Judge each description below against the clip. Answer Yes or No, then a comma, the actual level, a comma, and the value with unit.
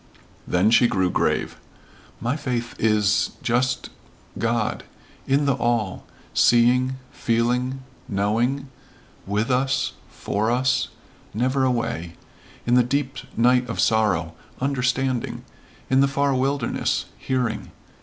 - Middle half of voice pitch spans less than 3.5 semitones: Yes, average, 2.8 semitones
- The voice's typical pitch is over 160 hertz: No, low, 125 Hz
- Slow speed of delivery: Yes, slow, 110 wpm